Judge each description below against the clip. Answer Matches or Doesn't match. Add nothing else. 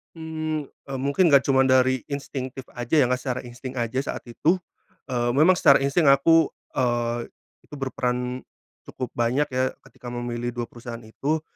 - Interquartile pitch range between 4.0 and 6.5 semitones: Doesn't match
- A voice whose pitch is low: Matches